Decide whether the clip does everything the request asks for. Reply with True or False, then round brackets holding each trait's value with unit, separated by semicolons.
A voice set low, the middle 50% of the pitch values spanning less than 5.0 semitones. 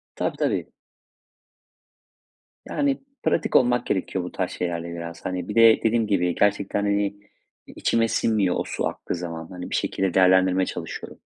True (95 Hz; 3.3 semitones)